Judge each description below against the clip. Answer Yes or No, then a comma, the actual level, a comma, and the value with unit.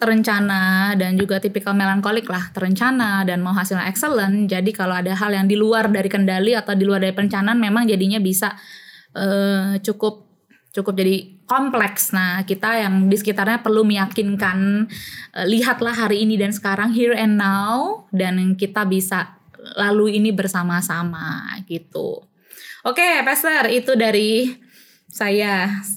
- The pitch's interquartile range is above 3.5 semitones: No, narrow, 2.5 semitones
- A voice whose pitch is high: Yes, high, 205 Hz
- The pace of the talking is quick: Yes, fast, 145 wpm